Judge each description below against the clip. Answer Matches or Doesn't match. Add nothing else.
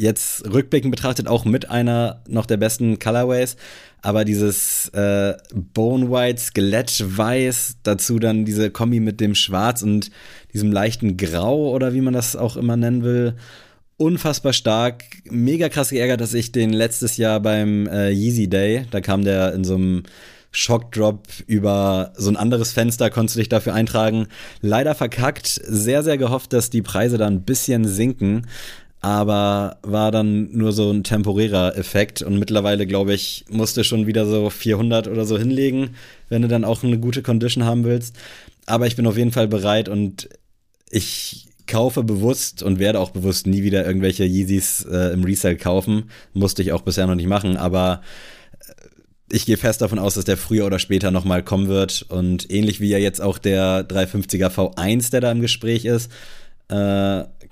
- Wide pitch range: Doesn't match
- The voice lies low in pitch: Matches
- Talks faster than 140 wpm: Matches